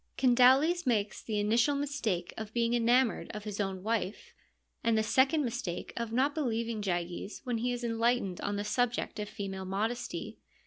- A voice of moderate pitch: No, high, 230 Hz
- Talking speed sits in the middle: Yes, average, 170 wpm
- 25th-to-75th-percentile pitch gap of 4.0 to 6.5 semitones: No, average, 3.2 semitones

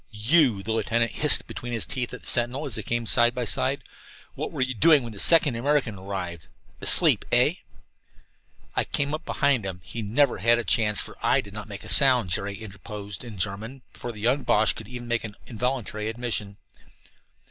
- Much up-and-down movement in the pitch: No, average, 3.3 semitones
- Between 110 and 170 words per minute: No, average, 200 wpm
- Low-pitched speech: Yes, low, 115 Hz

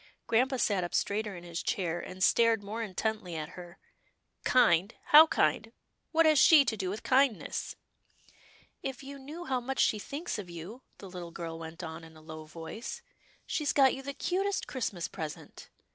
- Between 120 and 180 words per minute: No, fast, 205 wpm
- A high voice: Yes, high, 210 Hz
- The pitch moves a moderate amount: No, wide, 7.6 semitones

